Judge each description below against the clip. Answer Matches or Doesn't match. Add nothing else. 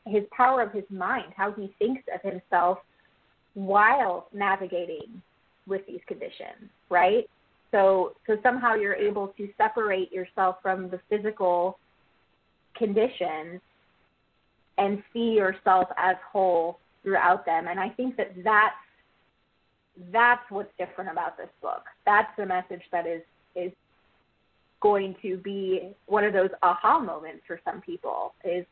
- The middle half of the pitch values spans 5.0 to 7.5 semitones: Doesn't match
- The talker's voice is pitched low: Doesn't match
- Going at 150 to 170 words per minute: Doesn't match